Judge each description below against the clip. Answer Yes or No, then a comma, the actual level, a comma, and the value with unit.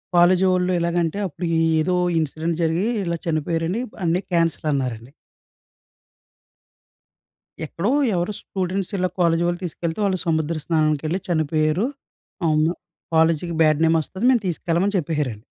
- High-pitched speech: No, medium, 165 Hz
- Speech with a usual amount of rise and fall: No, narrow, 2.3 semitones